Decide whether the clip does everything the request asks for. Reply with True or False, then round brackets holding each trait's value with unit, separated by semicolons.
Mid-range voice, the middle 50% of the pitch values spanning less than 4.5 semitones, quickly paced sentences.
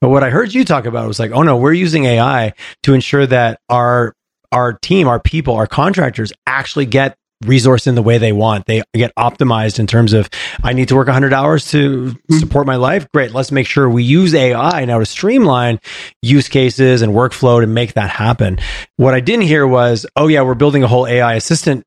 False (130 Hz; 3.3 semitones; 215 wpm)